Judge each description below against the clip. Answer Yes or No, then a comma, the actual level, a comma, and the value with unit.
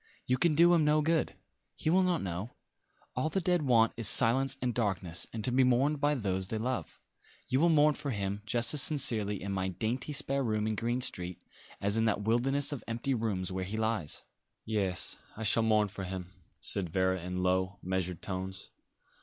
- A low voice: Yes, low, 110 Hz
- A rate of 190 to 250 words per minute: Yes, average, 200 wpm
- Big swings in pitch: Yes, wide, 6.1 semitones